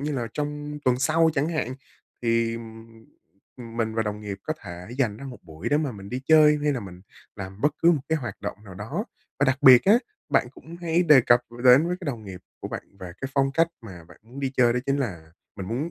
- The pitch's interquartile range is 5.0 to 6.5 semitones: Yes, wide, 5.6 semitones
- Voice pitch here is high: No, low, 125 Hz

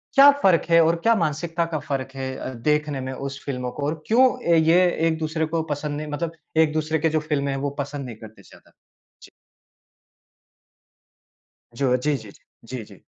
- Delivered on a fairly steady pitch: No, average, 3.1 semitones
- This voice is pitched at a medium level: Yes, medium, 150 Hz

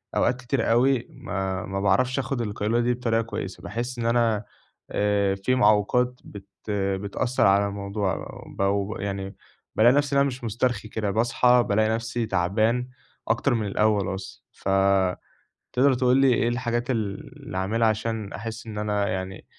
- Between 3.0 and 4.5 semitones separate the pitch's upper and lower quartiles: Yes, average, 3.3 semitones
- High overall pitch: No, low, 110 Hz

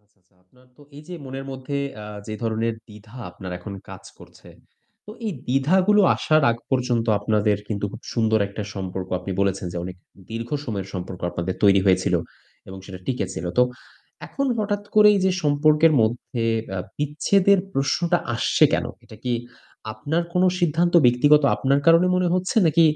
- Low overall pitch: Yes, low, 125 Hz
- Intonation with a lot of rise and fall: Yes, wide, 7.9 semitones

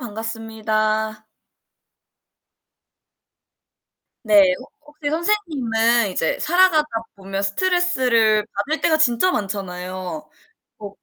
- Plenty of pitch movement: Yes, wide, 6.9 semitones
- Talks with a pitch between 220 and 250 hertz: Yes, high, 225 Hz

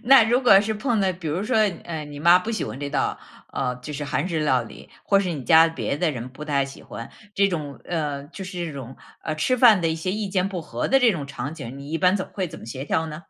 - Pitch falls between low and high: Yes, medium, 160 Hz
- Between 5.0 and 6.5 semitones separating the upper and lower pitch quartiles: Yes, wide, 5.4 semitones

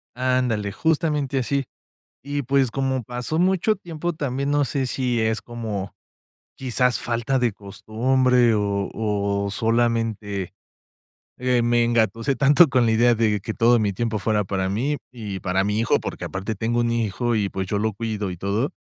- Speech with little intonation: No, average, 3.8 semitones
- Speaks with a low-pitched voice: Yes, low, 115 Hz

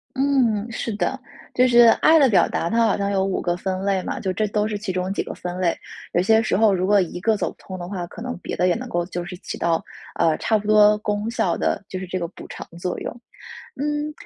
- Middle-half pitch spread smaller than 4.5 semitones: Yes, average, 3.9 semitones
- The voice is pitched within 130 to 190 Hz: No, high, 200 Hz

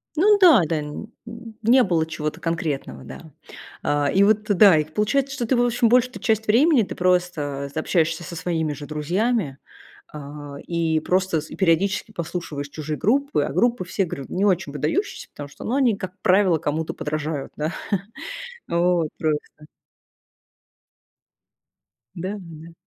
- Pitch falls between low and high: Yes, medium, 175 Hz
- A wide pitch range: Yes, wide, 6.0 semitones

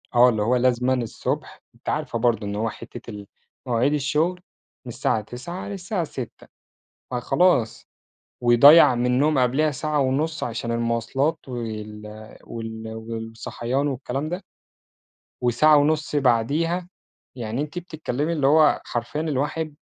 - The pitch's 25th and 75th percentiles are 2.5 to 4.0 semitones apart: No, average, 4.7 semitones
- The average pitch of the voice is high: No, low, 125 Hz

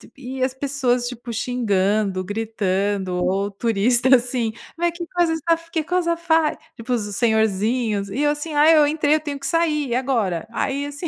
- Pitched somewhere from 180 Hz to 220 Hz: No, very high, 250 Hz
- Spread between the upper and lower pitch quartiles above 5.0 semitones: Yes, wide, 5.6 semitones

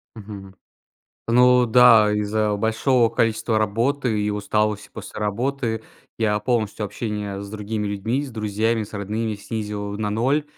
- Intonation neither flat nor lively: No, narrow, 1.9 semitones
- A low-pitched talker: Yes, low, 110 Hz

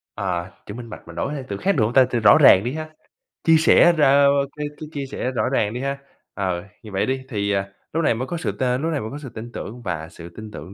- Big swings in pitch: Yes, wide, 5.9 semitones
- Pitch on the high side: No, low, 120 Hz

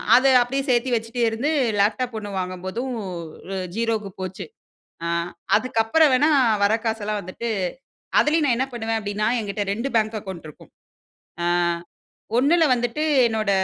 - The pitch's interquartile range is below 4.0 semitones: Yes, average, 3.5 semitones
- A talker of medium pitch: No, high, 225 Hz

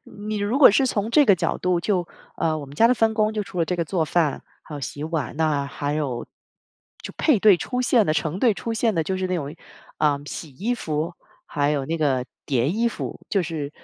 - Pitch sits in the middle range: Yes, medium, 170 Hz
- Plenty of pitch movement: Yes, wide, 6.2 semitones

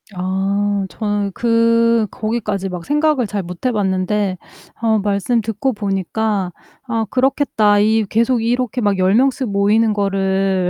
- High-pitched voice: Yes, high, 210 Hz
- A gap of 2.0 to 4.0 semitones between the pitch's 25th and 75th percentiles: Yes, average, 2.8 semitones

